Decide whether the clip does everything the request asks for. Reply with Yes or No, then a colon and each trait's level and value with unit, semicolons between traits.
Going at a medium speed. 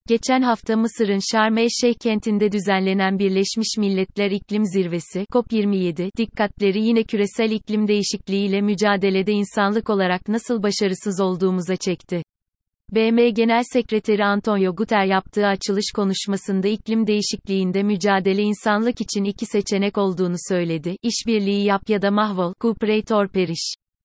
Yes: average, 120 wpm